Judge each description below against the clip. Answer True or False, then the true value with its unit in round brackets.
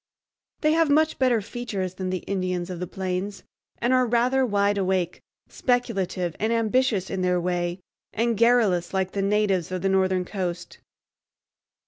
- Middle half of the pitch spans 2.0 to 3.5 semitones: False (4.3 semitones)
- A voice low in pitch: False (195 Hz)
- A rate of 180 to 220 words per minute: False (155 wpm)